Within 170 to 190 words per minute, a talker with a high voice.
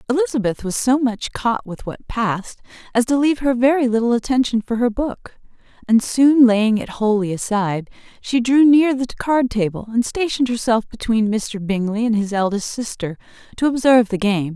Yes: average, 180 wpm; high, 230 Hz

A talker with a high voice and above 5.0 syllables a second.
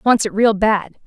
No: high, 210 Hz; 4.6 syllables/s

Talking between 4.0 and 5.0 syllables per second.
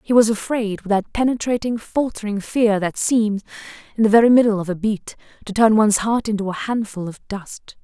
No: 5.4 syllables/s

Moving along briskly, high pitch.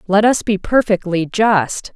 No: average, 155 wpm; high, 200 Hz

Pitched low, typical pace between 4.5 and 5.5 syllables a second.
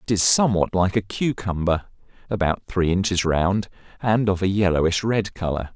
Yes: very low, 95 Hz; 5.1 syllables/s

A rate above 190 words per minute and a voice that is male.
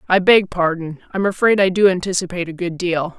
No: fast, 205 wpm; female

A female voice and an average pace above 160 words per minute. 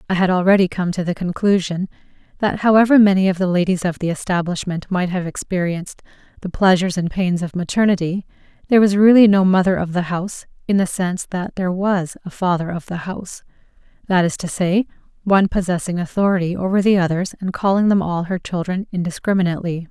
Yes: female; average, 185 wpm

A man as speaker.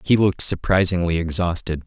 Yes: male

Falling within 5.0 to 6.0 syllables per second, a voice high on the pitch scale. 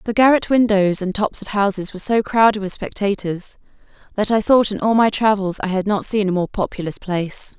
Yes: 5.5 syllables/s; high, 205 Hz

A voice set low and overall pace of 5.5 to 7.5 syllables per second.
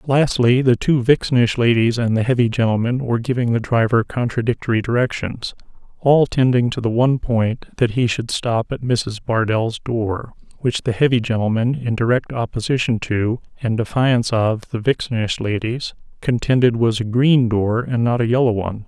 No: low, 120 Hz; 5.1 syllables/s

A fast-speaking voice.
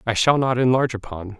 Yes: fast, 215 wpm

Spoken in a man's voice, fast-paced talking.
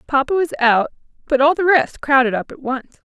No: female; fast, 210 wpm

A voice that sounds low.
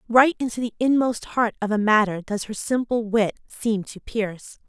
No: high, 220 Hz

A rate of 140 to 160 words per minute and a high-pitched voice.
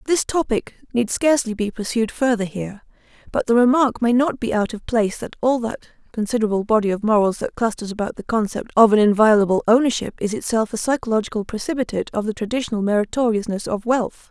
No: average, 185 wpm; high, 225 Hz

